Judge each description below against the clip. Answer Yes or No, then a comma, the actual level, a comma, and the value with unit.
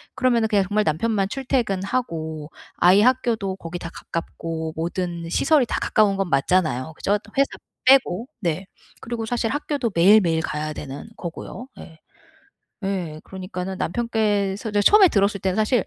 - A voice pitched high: Yes, high, 195 Hz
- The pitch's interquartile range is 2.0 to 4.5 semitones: No, average, 5.2 semitones